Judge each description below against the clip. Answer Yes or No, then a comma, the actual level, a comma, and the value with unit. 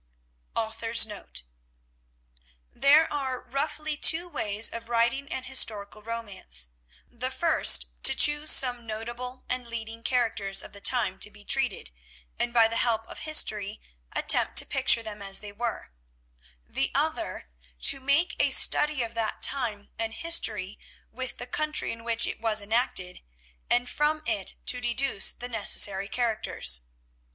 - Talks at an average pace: Yes, average, 145 wpm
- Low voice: No, high, 230 Hz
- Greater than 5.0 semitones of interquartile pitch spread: No, average, 3.6 semitones